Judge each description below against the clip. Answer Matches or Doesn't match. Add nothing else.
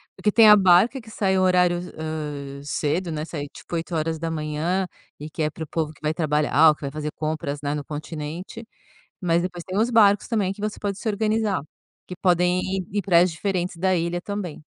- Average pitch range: Matches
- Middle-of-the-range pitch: Matches